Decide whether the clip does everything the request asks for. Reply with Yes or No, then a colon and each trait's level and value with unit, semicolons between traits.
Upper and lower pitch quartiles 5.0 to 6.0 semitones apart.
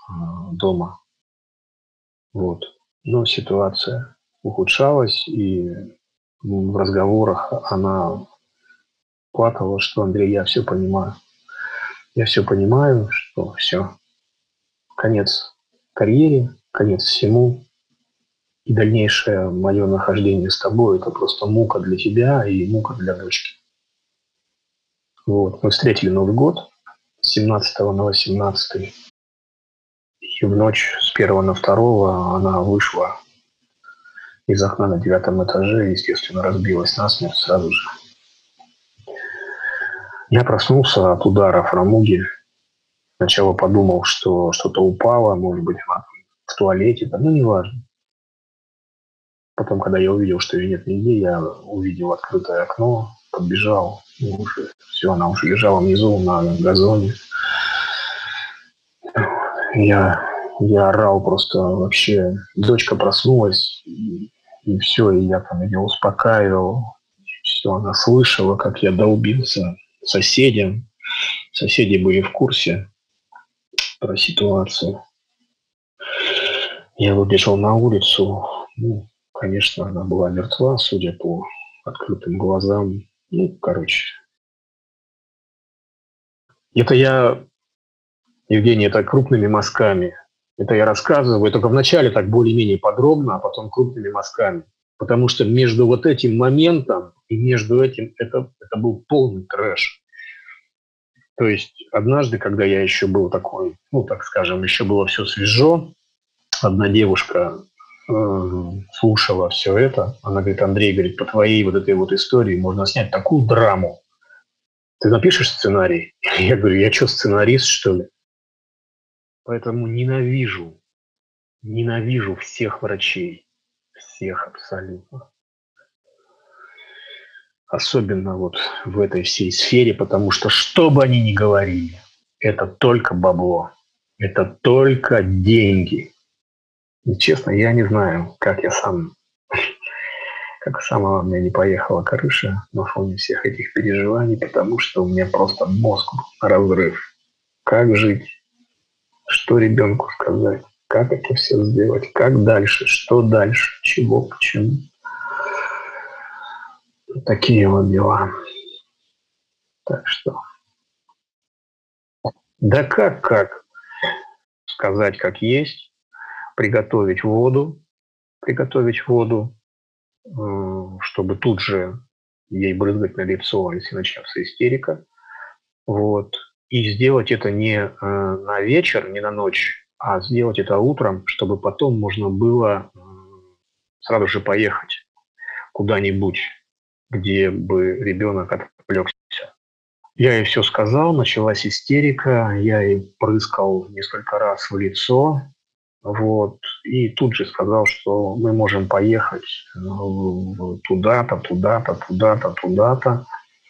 Yes: wide, 5.4 semitones